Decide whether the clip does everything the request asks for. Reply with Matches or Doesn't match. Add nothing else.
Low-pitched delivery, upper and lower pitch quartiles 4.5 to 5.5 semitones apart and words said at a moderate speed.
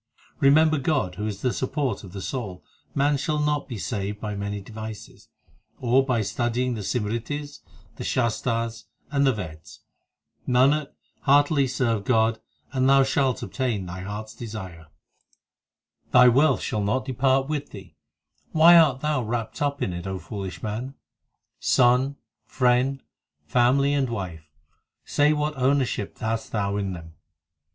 Matches